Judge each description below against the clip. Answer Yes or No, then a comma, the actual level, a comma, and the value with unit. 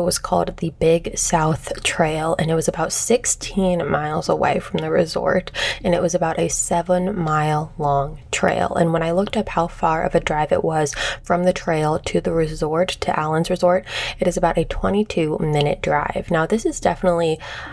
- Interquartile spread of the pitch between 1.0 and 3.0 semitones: Yes, narrow, 2.5 semitones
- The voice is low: No, medium, 170 Hz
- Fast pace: No, average, 195 wpm